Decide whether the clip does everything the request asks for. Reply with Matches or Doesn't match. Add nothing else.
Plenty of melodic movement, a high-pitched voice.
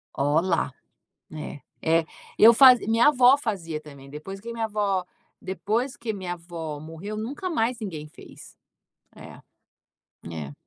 Matches